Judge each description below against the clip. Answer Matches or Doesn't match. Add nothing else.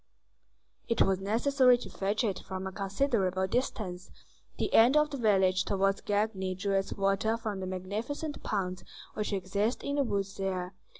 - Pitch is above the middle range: Matches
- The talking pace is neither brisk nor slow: Matches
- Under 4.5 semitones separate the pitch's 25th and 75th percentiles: Matches